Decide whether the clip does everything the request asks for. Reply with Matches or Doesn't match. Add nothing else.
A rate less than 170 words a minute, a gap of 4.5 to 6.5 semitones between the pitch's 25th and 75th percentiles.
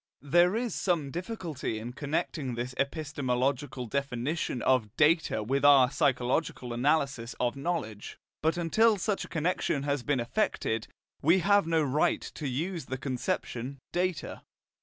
Matches